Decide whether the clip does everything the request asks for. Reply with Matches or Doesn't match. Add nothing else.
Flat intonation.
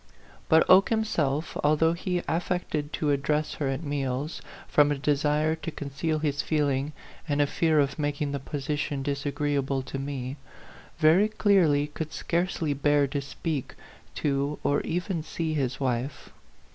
Matches